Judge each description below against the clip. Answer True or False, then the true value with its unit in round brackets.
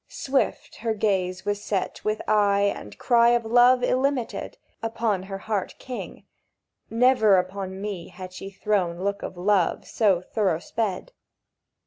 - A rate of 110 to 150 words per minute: True (140 wpm)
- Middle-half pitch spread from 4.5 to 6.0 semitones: False (3.3 semitones)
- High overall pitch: True (205 Hz)